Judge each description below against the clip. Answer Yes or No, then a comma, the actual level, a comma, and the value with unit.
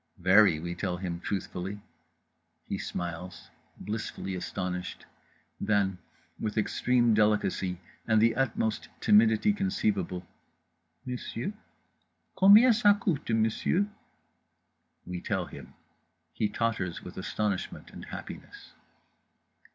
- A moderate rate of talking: No, slow, 100 wpm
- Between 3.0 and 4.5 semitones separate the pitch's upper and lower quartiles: Yes, average, 4.1 semitones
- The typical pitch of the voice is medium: No, low, 105 Hz